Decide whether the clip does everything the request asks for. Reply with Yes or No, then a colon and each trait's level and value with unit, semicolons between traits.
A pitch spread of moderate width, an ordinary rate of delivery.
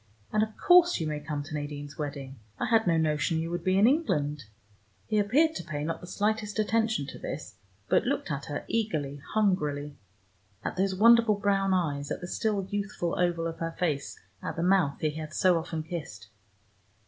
No: wide, 5.7 semitones; average, 195 wpm